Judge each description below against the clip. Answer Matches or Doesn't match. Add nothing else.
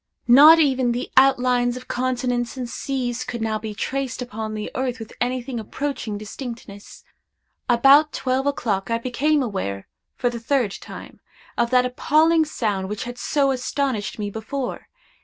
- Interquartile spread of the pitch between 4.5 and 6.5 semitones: Doesn't match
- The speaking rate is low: Doesn't match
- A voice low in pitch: Doesn't match